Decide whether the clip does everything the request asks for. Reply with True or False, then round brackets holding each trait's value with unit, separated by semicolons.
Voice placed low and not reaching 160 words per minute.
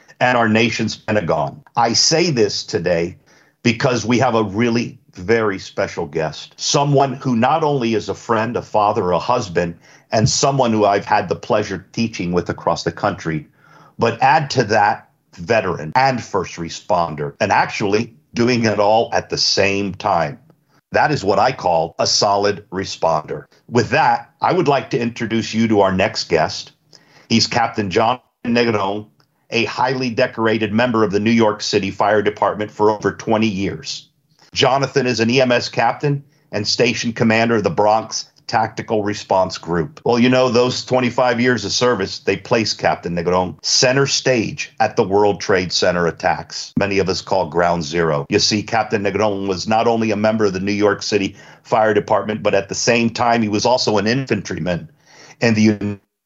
False (110 Hz; 175 wpm)